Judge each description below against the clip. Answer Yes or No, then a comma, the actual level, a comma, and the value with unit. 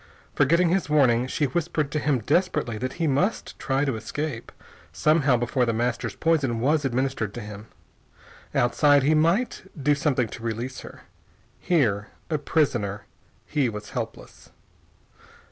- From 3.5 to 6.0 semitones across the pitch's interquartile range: Yes, average, 4.4 semitones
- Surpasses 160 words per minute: No, average, 145 wpm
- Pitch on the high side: No, low, 135 Hz